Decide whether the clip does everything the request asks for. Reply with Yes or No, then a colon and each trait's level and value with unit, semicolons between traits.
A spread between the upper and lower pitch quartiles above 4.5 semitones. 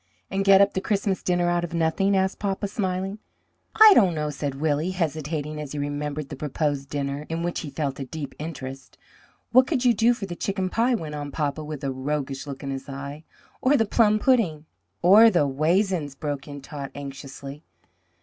Yes: average, 5.2 semitones